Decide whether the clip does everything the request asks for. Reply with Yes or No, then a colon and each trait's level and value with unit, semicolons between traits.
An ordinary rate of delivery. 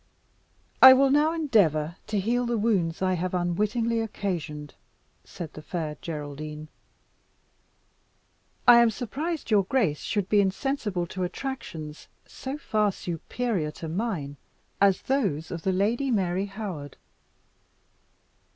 No: slow, 125 wpm